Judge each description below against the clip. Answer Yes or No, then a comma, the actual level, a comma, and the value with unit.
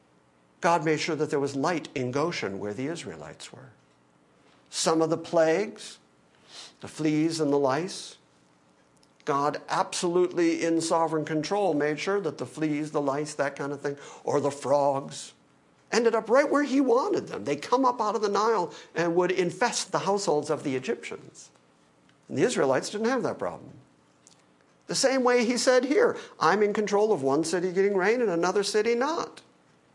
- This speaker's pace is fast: No, average, 175 wpm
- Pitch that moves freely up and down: Yes, wide, 7.9 semitones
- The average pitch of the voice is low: No, medium, 155 Hz